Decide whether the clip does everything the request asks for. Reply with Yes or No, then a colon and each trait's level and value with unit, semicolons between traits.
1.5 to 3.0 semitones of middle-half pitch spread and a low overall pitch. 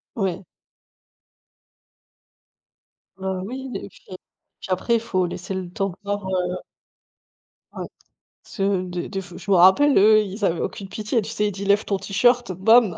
No: narrow, 2.5 semitones; high, 195 Hz